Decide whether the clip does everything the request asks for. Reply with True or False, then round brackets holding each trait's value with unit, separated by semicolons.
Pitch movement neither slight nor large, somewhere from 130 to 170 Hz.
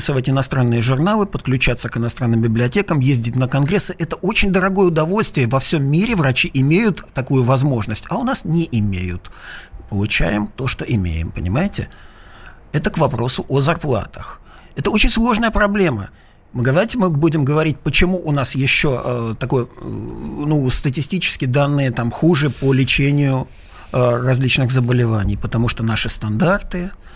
False (5.9 semitones; 135 Hz)